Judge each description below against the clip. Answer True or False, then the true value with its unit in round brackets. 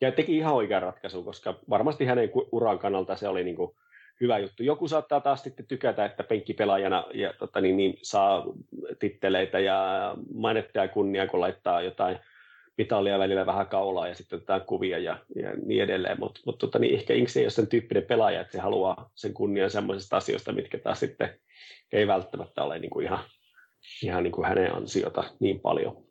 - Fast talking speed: True (180 wpm)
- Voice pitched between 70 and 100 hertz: False (130 Hz)